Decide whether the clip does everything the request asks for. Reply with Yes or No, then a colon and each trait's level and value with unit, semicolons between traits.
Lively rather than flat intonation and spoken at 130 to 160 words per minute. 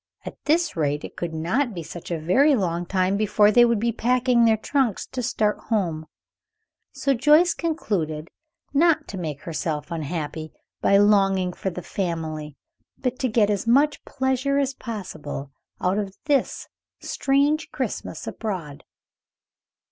Yes: wide, 7.5 semitones; average, 150 wpm